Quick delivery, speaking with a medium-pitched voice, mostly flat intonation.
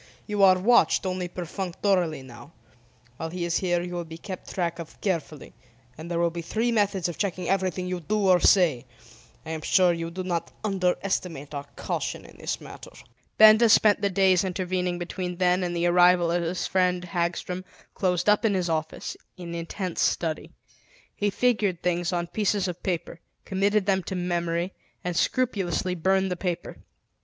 No: average, 175 wpm; medium, 180 Hz; narrow, 2.0 semitones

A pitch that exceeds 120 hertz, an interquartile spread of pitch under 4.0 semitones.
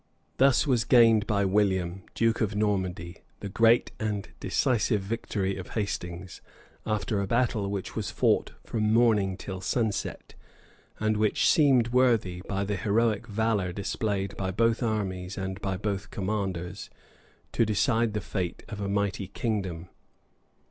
No: low, 105 Hz; average, 2.8 semitones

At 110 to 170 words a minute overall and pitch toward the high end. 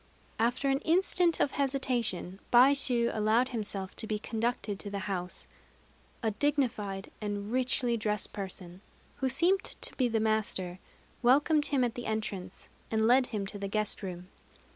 Yes: average, 155 wpm; high, 220 Hz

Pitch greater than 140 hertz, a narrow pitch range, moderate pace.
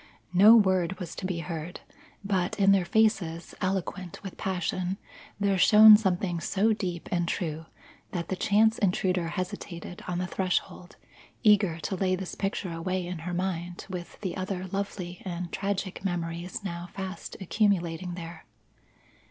Yes: medium, 185 Hz; narrow, 2.1 semitones; average, 150 wpm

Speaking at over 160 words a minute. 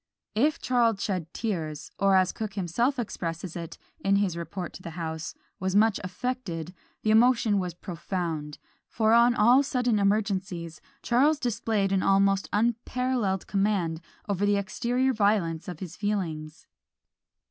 No: average, 140 wpm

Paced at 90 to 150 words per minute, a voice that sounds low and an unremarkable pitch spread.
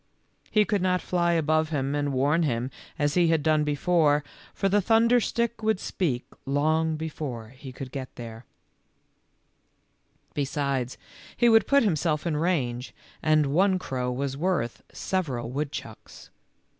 No: average, 145 wpm; medium, 155 Hz; average, 4.9 semitones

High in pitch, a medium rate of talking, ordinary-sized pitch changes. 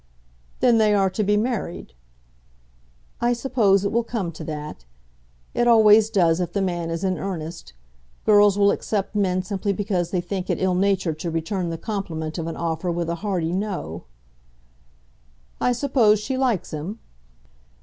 Yes: high, 195 Hz; average, 165 wpm; average, 3.8 semitones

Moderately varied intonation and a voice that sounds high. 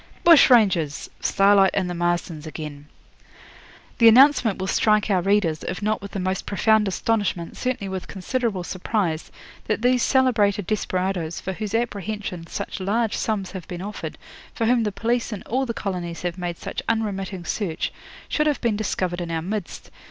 Yes: average, 3.8 semitones; high, 200 Hz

